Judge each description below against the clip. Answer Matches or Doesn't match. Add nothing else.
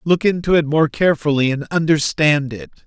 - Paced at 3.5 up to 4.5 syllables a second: Doesn't match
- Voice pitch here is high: Doesn't match